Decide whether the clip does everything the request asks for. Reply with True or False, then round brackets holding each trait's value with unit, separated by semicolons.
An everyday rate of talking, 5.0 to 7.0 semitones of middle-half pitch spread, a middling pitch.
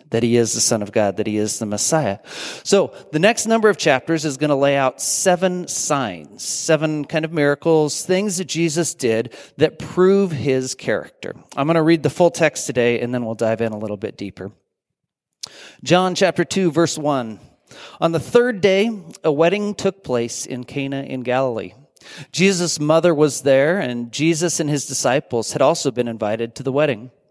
True (190 wpm; 5.6 semitones; 145 Hz)